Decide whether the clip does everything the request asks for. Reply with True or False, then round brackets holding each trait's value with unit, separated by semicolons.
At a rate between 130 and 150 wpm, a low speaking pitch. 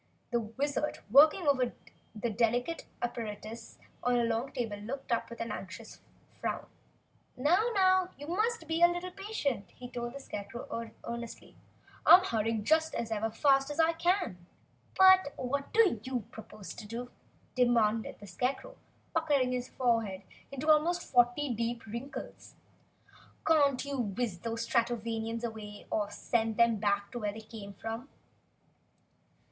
False (145 wpm; 240 Hz)